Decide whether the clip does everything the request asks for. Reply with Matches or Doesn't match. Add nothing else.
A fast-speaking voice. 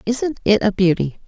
Doesn't match